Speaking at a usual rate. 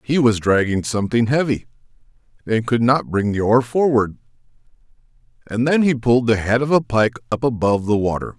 Yes: average, 180 wpm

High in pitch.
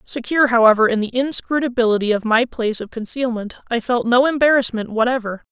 Yes: high, 240 Hz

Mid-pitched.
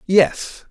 No: high, 195 Hz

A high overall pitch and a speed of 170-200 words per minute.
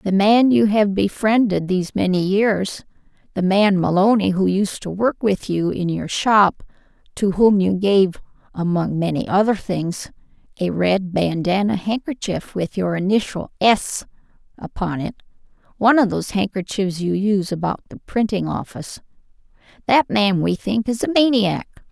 No: high, 200 Hz; average, 145 wpm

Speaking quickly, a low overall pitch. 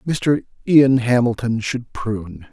No: slow, 120 wpm; low, 120 Hz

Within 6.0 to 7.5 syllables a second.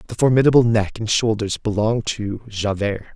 No: 5.4 syllables/s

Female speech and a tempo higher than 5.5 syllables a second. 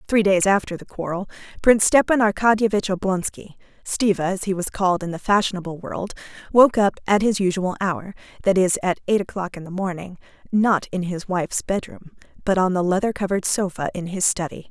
Yes: female; 5.7 syllables/s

